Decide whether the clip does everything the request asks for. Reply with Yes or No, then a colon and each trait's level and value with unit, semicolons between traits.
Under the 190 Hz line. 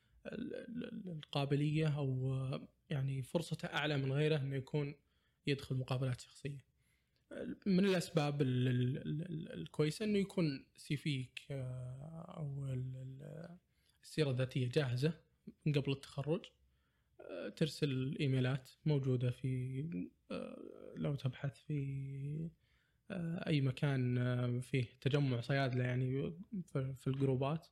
Yes: medium, 140 Hz